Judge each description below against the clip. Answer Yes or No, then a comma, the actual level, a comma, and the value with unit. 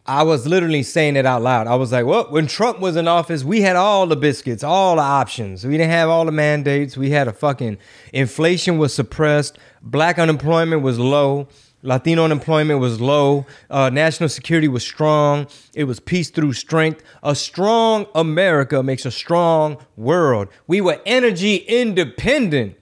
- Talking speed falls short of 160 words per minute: No, average, 175 wpm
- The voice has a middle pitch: Yes, medium, 150 Hz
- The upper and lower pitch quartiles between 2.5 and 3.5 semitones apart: Yes, average, 3.2 semitones